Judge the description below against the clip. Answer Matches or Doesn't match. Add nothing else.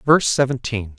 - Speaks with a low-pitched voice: Matches